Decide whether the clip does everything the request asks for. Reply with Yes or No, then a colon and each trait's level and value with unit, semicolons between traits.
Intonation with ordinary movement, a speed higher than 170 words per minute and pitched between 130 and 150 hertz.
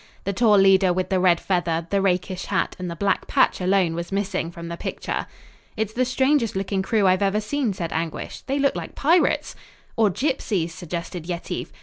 No: average, 3.2 semitones; average, 195 wpm; high, 190 Hz